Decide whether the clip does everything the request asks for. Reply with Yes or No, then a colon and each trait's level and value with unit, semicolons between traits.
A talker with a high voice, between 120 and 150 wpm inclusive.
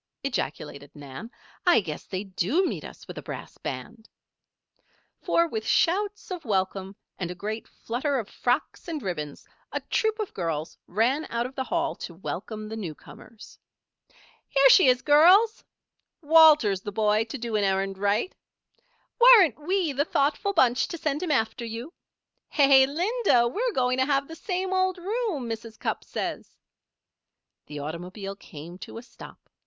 No: very high, 250 Hz; average, 160 wpm